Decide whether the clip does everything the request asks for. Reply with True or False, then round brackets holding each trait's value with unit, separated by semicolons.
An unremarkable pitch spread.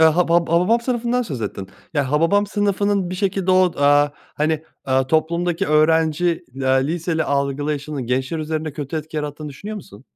True (3.7 semitones)